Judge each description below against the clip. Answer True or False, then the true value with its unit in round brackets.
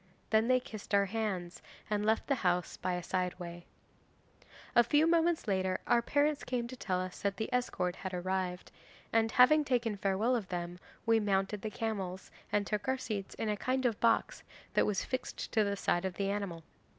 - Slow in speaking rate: False (200 wpm)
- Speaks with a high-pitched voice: True (210 Hz)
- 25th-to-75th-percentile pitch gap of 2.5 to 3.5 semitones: False (4.2 semitones)